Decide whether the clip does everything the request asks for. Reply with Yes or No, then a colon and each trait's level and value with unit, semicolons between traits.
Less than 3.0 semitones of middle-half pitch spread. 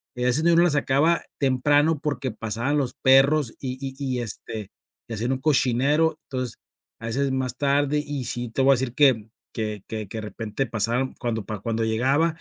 No: average, 3.8 semitones